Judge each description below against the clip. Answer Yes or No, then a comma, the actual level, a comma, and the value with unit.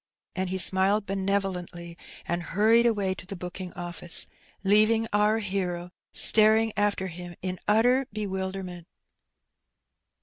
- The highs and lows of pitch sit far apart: No, average, 2.9 semitones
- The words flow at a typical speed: No, slow, 115 wpm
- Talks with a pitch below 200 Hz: Yes, high, 190 Hz